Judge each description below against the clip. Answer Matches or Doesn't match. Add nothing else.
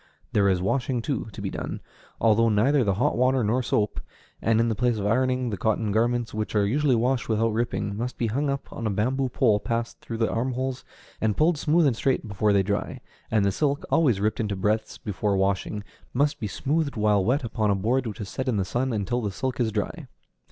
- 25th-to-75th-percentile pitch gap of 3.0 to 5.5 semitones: Matches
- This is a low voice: Matches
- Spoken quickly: Matches